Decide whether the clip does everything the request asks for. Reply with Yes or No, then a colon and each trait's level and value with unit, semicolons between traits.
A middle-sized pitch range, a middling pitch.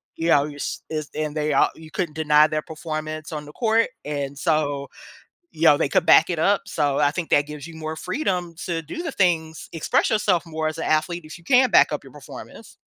No: narrow, 2.2 semitones; medium, 155 Hz